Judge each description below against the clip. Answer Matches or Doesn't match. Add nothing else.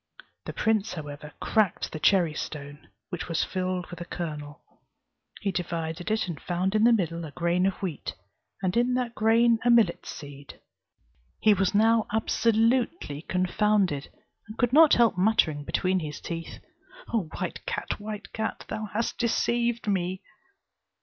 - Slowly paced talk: Doesn't match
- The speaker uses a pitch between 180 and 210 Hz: Matches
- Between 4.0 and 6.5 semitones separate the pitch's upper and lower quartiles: Matches